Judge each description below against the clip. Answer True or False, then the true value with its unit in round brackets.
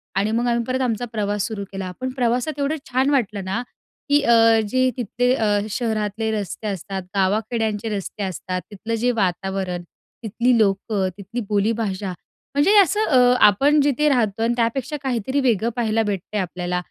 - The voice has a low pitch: False (225 Hz)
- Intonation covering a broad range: False (3.7 semitones)